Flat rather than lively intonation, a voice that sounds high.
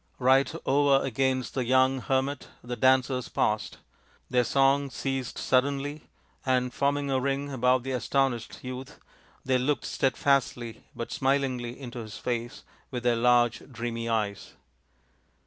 No: narrow, 2.0 semitones; low, 130 Hz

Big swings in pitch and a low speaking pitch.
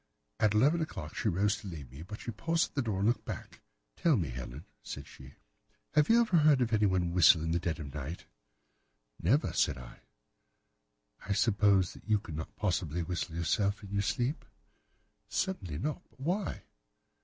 Yes: wide, 6.7 semitones; low, 100 Hz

